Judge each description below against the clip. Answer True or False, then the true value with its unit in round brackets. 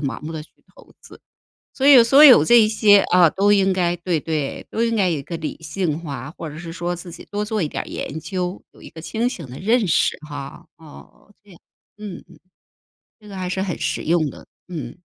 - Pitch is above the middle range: False (180 Hz)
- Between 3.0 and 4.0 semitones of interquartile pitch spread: False (4.5 semitones)